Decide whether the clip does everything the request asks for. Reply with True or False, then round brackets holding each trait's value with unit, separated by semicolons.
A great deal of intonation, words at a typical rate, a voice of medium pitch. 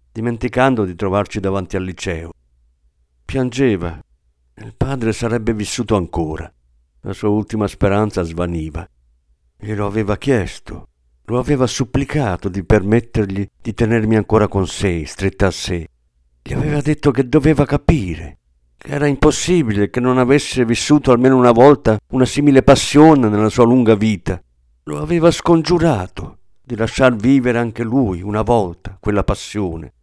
False (6.3 semitones; 135 wpm; 105 Hz)